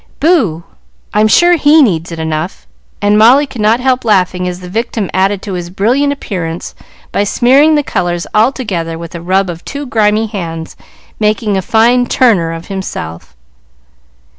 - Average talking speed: Yes, average, 165 wpm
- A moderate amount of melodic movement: No, wide, 5.7 semitones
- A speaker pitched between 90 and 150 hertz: No, high, 205 Hz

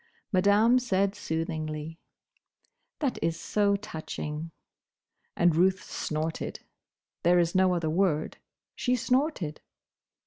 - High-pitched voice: No, medium, 180 Hz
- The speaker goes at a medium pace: No, slow, 100 wpm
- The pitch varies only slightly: No, average, 4.1 semitones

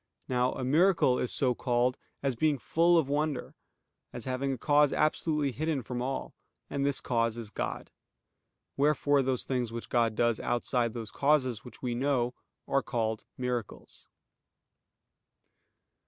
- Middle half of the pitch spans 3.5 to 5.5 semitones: No, average, 3.0 semitones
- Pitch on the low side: Yes, low, 130 Hz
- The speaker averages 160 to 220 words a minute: No, average, 145 wpm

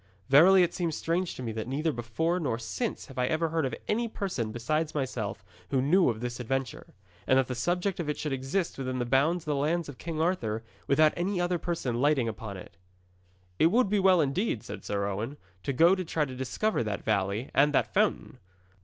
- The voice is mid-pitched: Yes, medium, 145 Hz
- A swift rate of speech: Yes, fast, 215 wpm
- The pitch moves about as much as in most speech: No, wide, 5.9 semitones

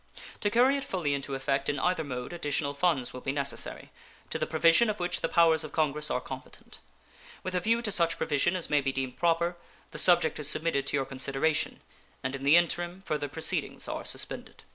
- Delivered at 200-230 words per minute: Yes, fast, 205 wpm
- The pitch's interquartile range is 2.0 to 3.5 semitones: No, average, 4.0 semitones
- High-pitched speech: No, medium, 155 Hz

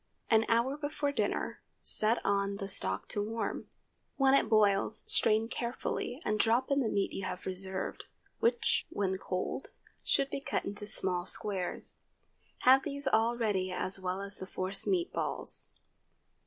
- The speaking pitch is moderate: No, high, 215 Hz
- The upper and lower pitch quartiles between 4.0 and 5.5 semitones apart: Yes, average, 4.5 semitones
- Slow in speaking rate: No, average, 155 wpm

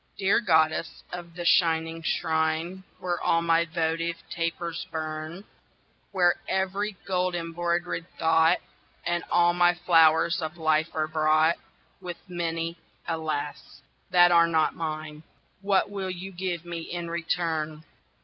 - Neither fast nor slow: No, slow, 130 wpm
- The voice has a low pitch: No, medium, 170 Hz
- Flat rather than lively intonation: Yes, narrow, 1.6 semitones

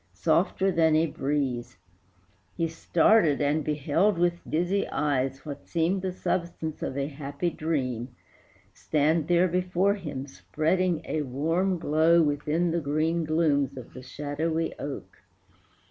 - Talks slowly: Yes, slow, 130 wpm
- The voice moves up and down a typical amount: Yes, average, 3.2 semitones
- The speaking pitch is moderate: Yes, medium, 155 Hz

